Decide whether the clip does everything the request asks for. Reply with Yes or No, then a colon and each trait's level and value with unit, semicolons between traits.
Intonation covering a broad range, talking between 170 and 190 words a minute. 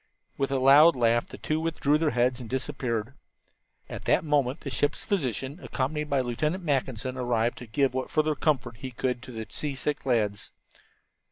No: average, 3.5 semitones; average, 175 wpm